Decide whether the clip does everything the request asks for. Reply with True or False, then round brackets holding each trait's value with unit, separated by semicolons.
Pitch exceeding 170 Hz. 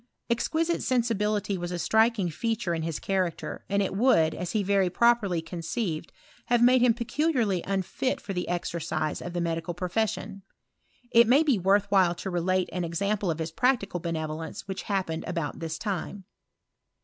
True (190 Hz)